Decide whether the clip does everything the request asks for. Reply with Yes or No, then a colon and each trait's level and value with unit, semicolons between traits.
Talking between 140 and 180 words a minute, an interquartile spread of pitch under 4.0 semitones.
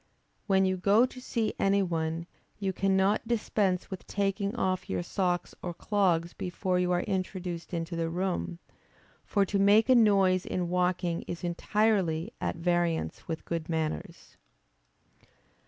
Yes: average, 145 wpm; narrow, 2.6 semitones